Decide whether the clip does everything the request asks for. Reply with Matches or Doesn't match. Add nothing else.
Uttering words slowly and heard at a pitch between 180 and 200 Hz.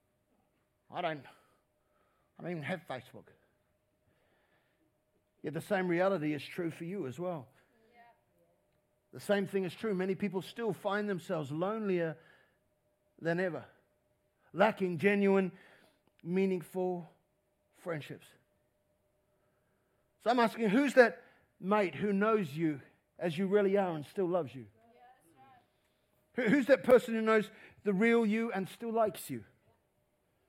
Matches